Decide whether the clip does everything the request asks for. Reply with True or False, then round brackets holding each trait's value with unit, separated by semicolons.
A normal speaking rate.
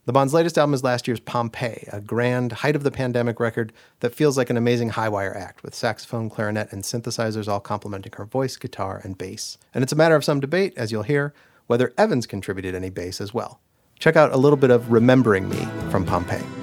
False (225 wpm)